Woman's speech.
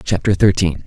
No: male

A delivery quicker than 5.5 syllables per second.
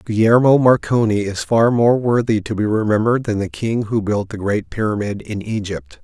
No: 5.0 syllables/s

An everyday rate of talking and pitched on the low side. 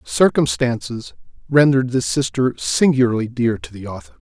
No: slow, 125 wpm; low, 115 Hz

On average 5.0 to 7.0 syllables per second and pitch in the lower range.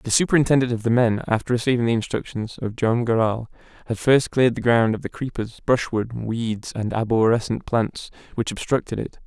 Yes: 5.5 syllables/s; low, 120 Hz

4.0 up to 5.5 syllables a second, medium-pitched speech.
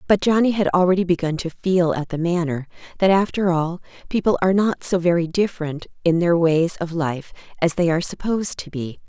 No: 5.7 syllables/s; medium, 175 Hz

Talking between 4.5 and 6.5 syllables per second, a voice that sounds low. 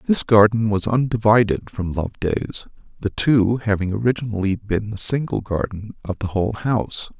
Yes: 5.0 syllables/s; low, 105 Hz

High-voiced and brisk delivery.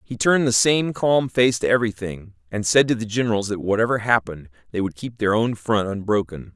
No: low, 110 Hz; fast, 210 wpm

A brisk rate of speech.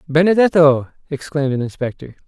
No: slow, 105 wpm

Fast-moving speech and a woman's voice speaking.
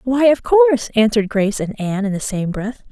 Yes: fast, 225 wpm; female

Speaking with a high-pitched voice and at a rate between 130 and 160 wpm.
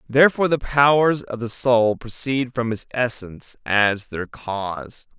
No: low, 120 Hz; average, 150 wpm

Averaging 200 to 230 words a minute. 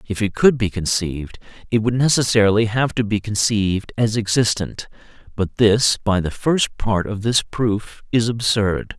No: average, 165 wpm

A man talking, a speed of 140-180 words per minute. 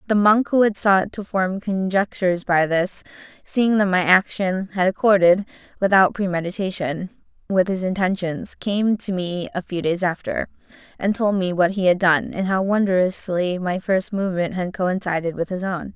No: female; average, 175 wpm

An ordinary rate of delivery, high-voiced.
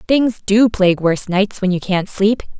No: fast, 210 wpm; high, 200 Hz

